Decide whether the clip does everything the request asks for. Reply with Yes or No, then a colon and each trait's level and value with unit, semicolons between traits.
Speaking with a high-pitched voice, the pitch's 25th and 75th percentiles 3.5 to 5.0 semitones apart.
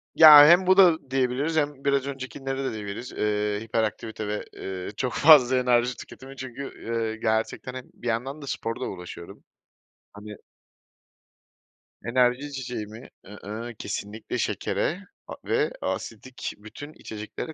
No: low, 125 Hz; average, 3.8 semitones